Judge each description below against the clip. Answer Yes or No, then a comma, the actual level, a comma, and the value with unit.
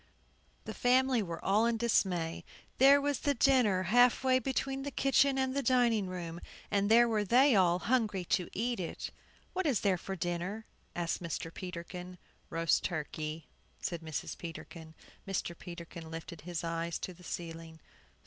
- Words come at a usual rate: Yes, average, 160 wpm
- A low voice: No, high, 190 Hz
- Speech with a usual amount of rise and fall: No, wide, 6.3 semitones